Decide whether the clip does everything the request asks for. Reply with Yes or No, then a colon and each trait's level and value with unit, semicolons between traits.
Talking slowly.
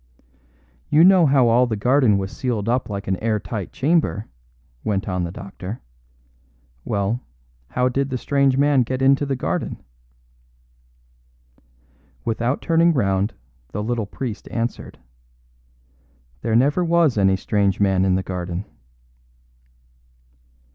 Yes: slow, 125 wpm